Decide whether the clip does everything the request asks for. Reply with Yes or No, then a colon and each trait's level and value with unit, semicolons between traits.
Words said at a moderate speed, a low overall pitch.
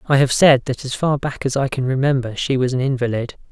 No: fast, 255 wpm; low, 130 Hz